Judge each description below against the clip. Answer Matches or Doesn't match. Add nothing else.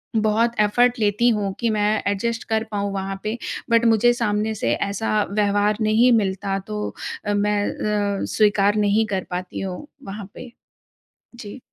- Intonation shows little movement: Matches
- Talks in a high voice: Matches